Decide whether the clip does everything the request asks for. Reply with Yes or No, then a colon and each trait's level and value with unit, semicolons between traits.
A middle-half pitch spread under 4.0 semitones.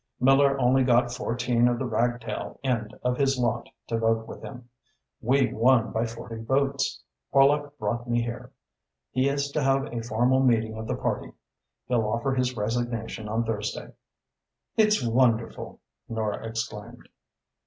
Yes: average, 2.7 semitones